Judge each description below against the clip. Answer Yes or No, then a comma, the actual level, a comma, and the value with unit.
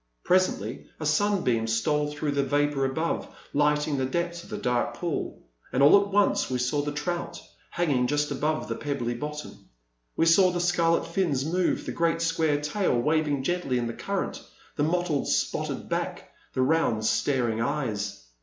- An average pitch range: Yes, average, 4.2 semitones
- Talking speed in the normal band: Yes, average, 175 wpm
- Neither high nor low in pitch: Yes, medium, 150 Hz